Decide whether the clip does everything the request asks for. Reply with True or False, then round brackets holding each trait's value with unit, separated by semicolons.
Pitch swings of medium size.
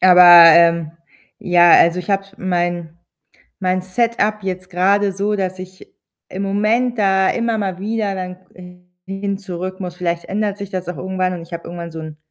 False (2.3 semitones)